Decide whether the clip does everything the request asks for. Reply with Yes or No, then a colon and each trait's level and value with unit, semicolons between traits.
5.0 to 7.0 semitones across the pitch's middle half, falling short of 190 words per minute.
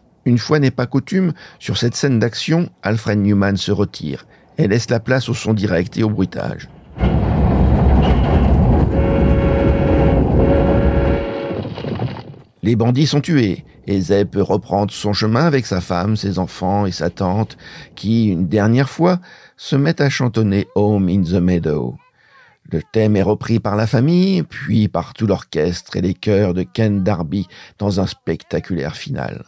No: average, 4.5 semitones; average, 150 wpm